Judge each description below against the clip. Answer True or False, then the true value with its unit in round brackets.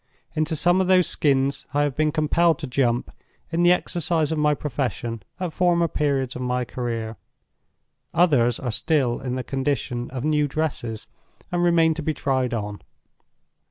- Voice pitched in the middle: True (145 Hz)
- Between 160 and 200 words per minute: True (165 wpm)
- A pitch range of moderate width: True (4.5 semitones)